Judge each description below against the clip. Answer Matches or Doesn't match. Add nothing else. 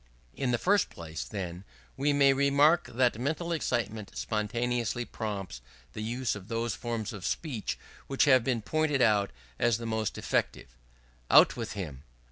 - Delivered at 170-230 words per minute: Doesn't match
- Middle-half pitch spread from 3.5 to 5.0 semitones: Matches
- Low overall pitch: Matches